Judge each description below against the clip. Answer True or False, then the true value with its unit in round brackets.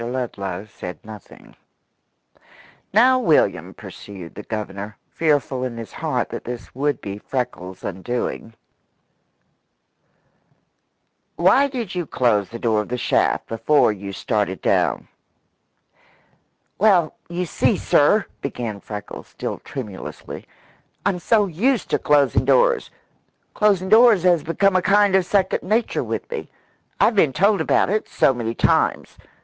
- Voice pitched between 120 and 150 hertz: True (140 Hz)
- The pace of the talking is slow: True (130 wpm)